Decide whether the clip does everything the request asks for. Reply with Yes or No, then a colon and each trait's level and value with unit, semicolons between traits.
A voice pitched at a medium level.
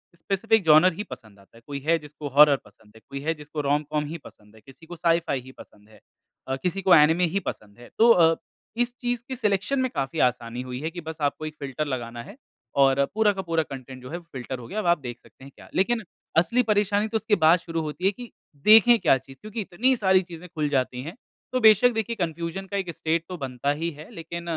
Yes: medium, 160 Hz